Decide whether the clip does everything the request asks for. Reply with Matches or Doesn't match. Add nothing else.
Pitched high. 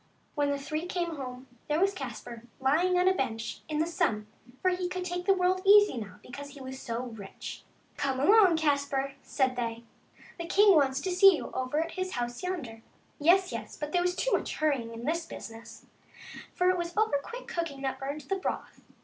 Matches